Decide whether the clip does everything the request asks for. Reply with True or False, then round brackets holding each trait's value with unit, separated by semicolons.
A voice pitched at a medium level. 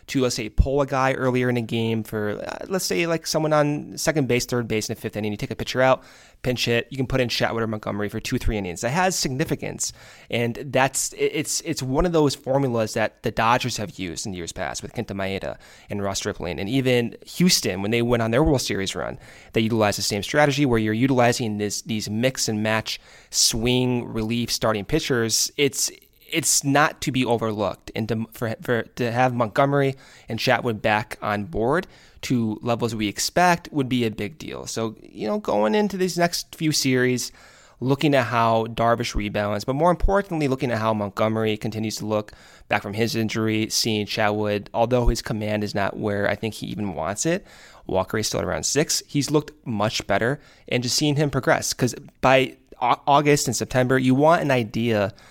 False (120 Hz)